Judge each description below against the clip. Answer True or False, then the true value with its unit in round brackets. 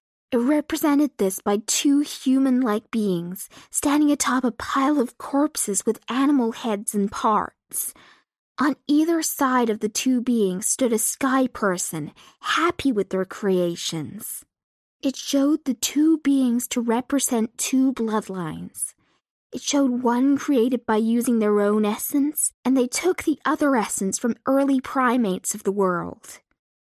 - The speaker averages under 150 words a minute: True (140 wpm)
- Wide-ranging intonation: False (4.8 semitones)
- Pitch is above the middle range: True (250 Hz)